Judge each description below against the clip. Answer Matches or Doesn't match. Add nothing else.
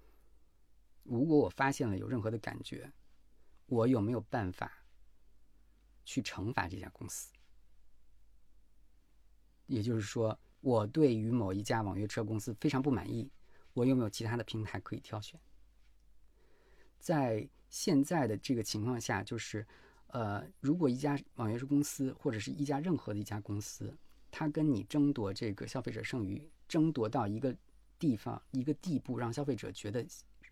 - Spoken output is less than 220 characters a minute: Doesn't match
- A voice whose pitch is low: Matches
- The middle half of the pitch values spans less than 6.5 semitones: Matches